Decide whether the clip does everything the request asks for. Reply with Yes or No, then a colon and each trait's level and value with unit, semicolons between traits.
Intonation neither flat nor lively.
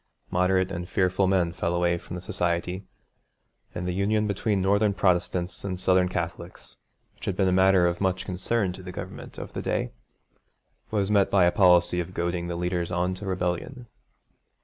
No: narrow, 1.6 semitones